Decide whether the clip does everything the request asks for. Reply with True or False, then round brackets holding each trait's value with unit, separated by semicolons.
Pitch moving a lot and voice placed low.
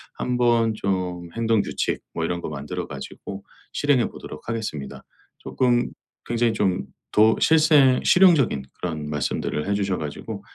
True (5.8 semitones; 105 Hz)